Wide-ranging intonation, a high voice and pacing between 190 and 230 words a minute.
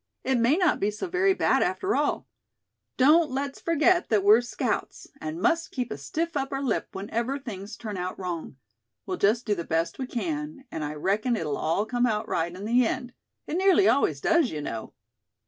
Yes: wide, 7.4 semitones; high, 240 Hz; average, 200 wpm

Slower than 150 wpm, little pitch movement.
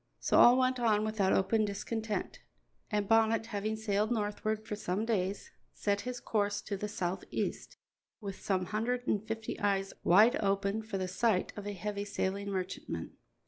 No: average, 165 wpm; narrow, 1.9 semitones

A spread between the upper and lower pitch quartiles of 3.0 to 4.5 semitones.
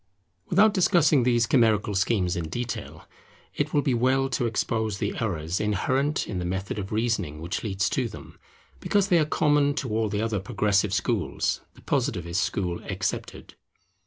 No: wide, 5.6 semitones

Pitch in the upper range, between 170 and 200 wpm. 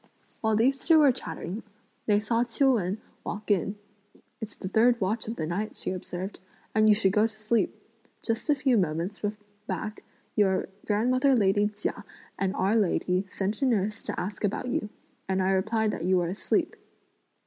Yes: high, 210 Hz; average, 180 wpm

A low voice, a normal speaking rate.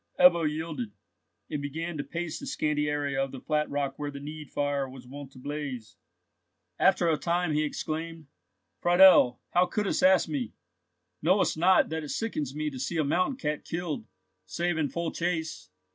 No: medium, 155 Hz; average, 175 wpm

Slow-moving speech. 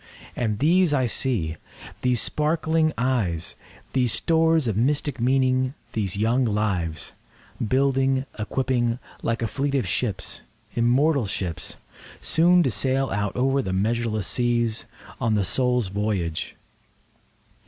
Yes: slow, 100 wpm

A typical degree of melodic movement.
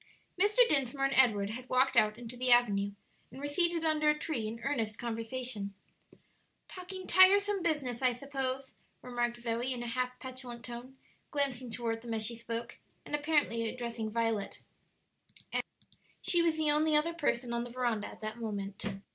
Yes: average, 4.0 semitones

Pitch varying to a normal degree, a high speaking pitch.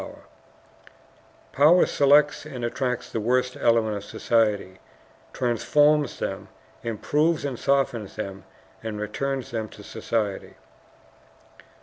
No: average, 4.4 semitones; low, 120 Hz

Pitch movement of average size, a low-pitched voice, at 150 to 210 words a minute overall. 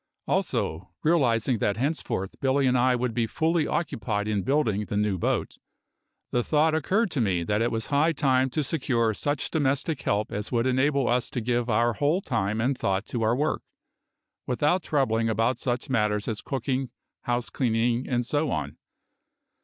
Yes: average, 4.1 semitones; low, 125 Hz; average, 175 wpm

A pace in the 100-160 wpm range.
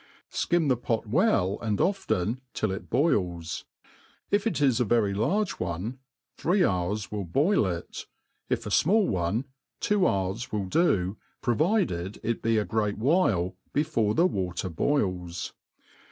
Yes: average, 145 wpm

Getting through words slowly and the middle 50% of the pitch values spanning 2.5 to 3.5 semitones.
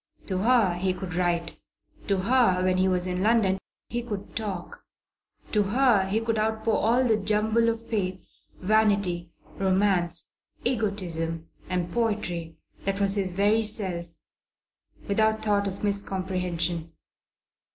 Yes: slow, 130 wpm; average, 3.1 semitones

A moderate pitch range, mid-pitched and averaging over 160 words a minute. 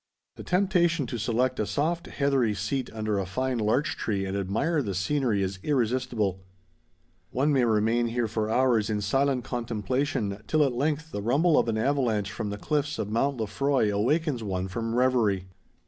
No: average, 5.0 semitones; low, 120 Hz; average, 175 wpm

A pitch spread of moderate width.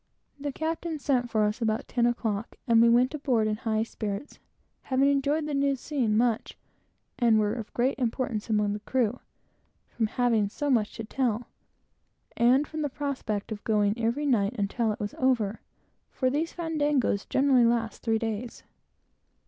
Yes: average, 4.0 semitones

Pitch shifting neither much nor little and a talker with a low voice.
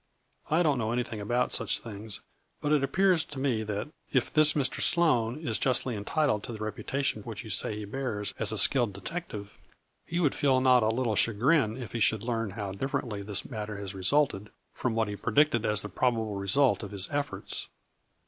Yes: average, 4.6 semitones; low, 115 Hz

